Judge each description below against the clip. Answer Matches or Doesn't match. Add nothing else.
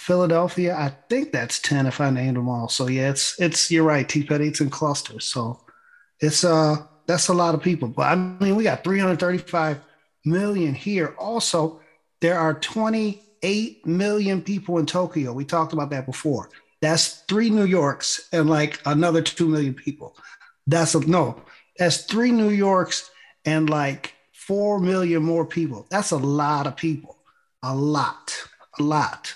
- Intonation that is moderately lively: Matches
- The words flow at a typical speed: Matches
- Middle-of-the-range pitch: Matches